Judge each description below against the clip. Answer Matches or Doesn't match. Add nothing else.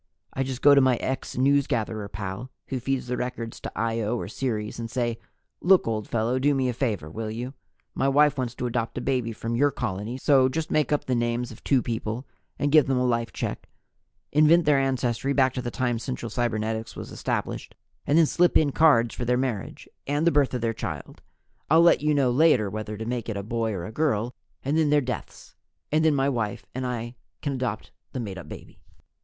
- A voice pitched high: Doesn't match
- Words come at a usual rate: Doesn't match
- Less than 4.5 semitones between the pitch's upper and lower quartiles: Matches